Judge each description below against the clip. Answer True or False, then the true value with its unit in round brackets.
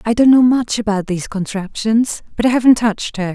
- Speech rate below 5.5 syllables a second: False (5.8 syllables/s)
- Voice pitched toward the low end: False (220 Hz)